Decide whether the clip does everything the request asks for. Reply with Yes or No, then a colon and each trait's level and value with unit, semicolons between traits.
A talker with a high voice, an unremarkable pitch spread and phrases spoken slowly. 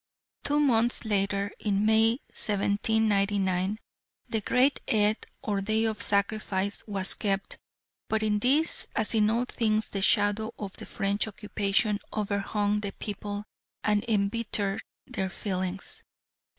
No: high, 210 Hz; narrow, 1.7 semitones; slow, 125 wpm